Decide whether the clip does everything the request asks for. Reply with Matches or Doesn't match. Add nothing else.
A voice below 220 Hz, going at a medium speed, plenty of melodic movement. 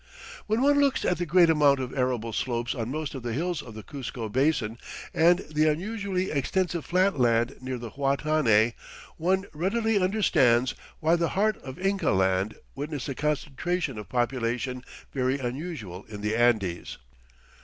Matches